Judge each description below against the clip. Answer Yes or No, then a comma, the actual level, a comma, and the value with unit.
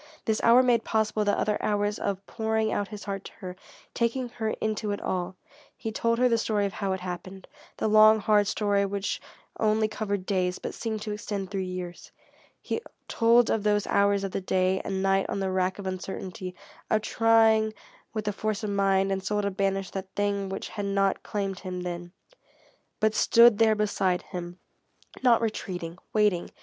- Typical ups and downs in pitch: No, narrow, 2.2 semitones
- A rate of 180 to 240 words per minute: Yes, average, 190 wpm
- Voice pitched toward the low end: No, high, 205 Hz